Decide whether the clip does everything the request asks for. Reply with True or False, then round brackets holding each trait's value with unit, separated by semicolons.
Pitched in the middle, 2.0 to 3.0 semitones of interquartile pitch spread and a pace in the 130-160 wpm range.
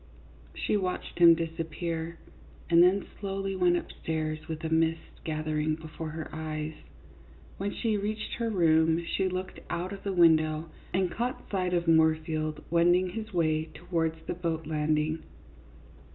True (165 Hz; 2.6 semitones; 150 wpm)